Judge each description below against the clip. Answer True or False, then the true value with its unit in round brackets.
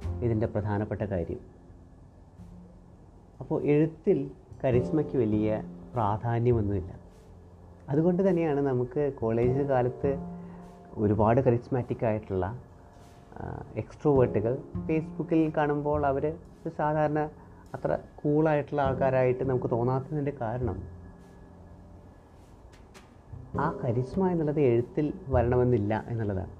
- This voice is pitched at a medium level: False (120 Hz)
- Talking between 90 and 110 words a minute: False (75 wpm)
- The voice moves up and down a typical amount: False (7.1 semitones)